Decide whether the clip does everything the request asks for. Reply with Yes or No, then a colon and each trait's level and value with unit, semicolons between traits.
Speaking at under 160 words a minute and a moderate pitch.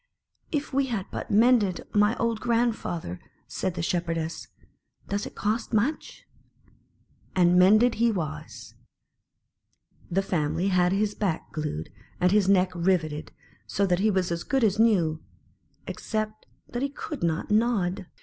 No: average, 145 wpm; high, 195 Hz